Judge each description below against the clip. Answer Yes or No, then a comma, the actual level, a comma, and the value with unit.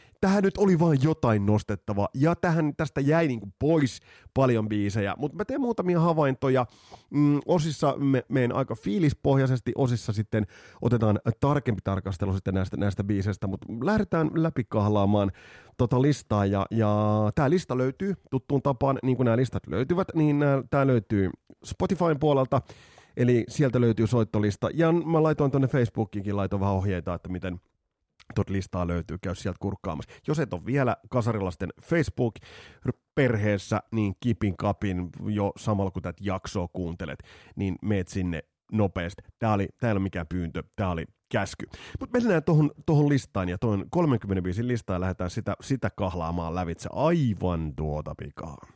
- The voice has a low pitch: Yes, low, 115 Hz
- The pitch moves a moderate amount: No, wide, 6.2 semitones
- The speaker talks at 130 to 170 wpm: Yes, average, 150 wpm